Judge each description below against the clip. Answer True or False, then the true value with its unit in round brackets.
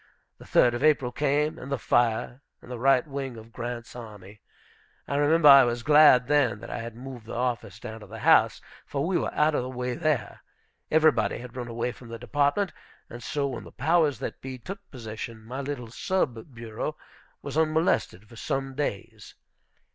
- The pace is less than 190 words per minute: False (195 wpm)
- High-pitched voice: False (125 Hz)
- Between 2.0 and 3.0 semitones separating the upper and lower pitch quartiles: False (3.8 semitones)